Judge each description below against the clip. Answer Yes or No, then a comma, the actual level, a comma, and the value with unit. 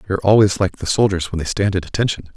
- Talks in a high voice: No, very low, 95 Hz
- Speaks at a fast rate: Yes, fast, 255 wpm